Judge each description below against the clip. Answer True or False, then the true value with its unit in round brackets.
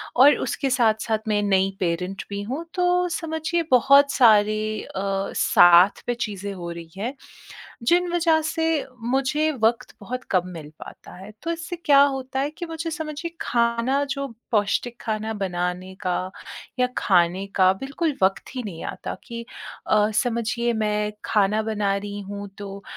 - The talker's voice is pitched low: False (220 Hz)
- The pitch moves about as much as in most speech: False (5.9 semitones)